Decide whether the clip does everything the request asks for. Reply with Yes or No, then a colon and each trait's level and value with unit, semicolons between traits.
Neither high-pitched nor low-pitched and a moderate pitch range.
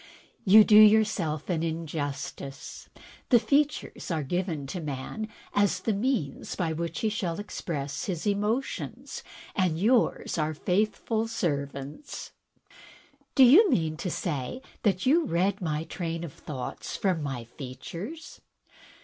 No: medium, 175 Hz; wide, 6.0 semitones